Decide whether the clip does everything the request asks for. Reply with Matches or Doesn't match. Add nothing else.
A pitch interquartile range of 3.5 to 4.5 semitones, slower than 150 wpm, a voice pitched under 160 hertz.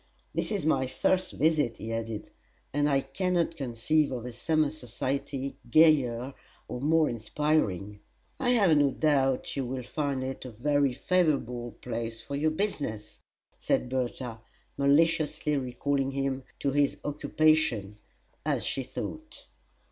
Matches